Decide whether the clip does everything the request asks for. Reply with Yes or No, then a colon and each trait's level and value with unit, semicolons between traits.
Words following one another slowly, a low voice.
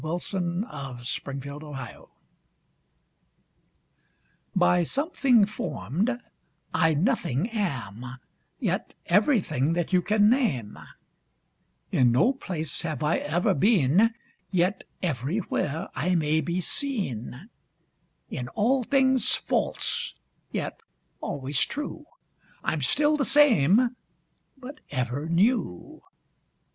No: slow, 100 wpm; medium, 175 Hz